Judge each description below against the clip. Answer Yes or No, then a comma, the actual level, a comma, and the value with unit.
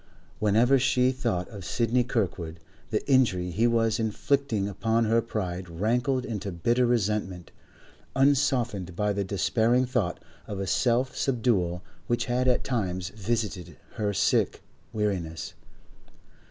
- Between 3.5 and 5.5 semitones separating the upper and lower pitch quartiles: Yes, average, 4.3 semitones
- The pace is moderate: No, slow, 125 wpm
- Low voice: Yes, low, 110 Hz